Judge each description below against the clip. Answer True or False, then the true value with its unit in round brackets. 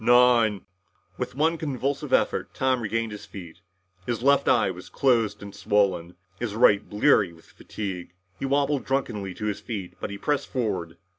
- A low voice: True (110 Hz)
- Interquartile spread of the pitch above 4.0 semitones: True (4.7 semitones)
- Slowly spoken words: False (170 wpm)